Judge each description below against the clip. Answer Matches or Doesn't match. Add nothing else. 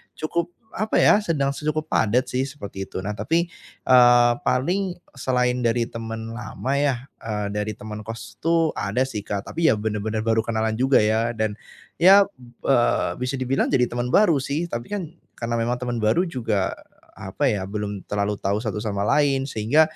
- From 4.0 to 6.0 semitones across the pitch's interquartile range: Matches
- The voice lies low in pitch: Matches